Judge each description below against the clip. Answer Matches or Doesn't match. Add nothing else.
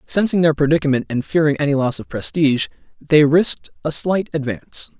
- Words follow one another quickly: Doesn't match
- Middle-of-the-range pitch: Matches